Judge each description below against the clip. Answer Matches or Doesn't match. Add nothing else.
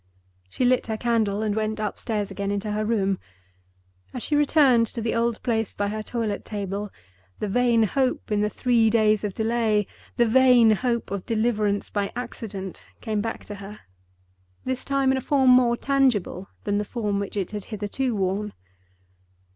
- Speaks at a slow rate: Doesn't match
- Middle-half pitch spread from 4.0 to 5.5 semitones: Doesn't match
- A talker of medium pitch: Doesn't match